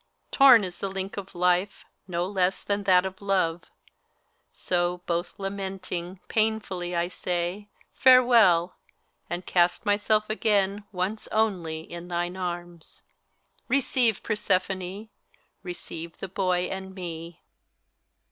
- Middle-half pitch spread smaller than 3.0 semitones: Yes, narrow, 2.6 semitones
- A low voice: No, medium, 185 Hz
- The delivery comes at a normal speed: No, slow, 120 wpm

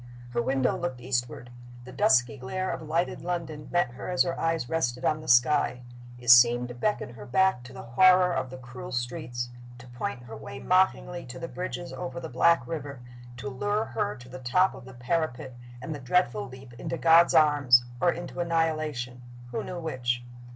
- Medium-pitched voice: No, low, 130 Hz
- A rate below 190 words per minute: No, average, 195 wpm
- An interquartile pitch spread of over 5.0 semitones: Yes, wide, 5.5 semitones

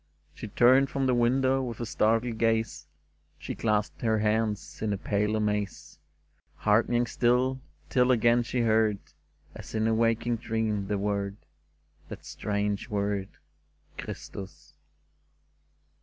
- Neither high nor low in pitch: No, low, 110 Hz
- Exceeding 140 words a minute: No, slow, 135 wpm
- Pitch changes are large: No, narrow, 2.5 semitones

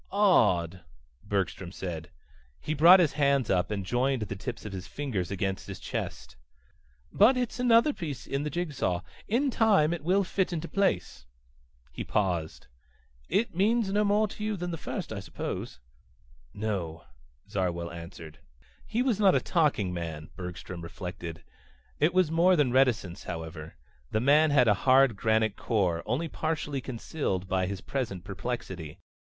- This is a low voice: Yes, low, 120 Hz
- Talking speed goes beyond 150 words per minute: Yes, average, 160 wpm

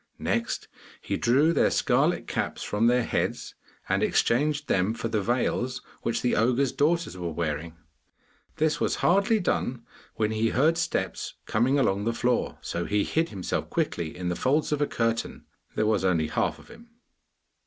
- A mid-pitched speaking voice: No, low, 120 Hz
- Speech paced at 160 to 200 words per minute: Yes, average, 170 wpm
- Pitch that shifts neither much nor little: No, wide, 6.0 semitones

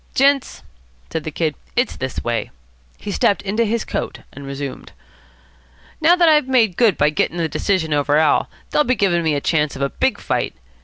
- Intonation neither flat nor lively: No, wide, 8.1 semitones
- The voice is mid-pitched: Yes, medium, 170 Hz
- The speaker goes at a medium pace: Yes, average, 195 wpm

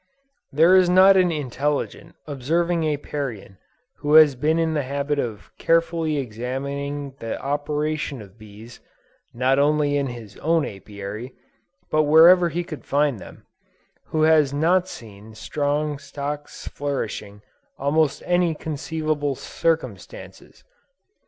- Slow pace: Yes, slow, 125 wpm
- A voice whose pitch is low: No, medium, 145 Hz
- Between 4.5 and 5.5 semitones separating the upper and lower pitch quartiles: No, average, 3.6 semitones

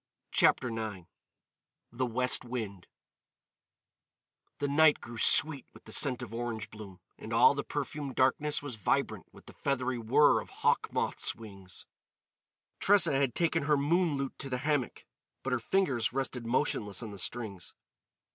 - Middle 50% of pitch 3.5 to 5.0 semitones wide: Yes, average, 4.3 semitones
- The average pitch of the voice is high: No, low, 125 Hz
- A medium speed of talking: Yes, average, 155 wpm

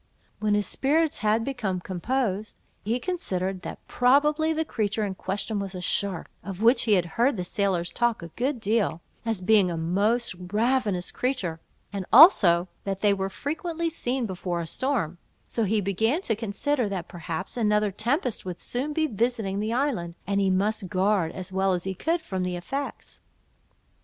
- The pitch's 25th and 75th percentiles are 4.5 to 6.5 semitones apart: Yes, average, 4.8 semitones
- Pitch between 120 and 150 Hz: No, high, 210 Hz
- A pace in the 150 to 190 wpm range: Yes, average, 175 wpm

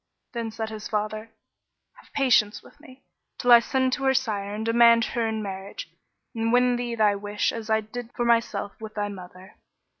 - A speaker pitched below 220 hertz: No, high, 225 Hz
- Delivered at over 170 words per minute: Yes, average, 190 wpm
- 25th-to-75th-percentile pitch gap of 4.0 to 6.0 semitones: No, narrow, 2.5 semitones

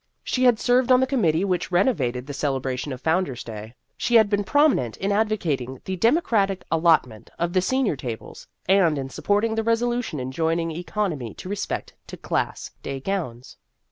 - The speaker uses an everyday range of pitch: No, wide, 8.3 semitones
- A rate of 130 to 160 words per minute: No, average, 175 wpm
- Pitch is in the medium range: Yes, medium, 180 Hz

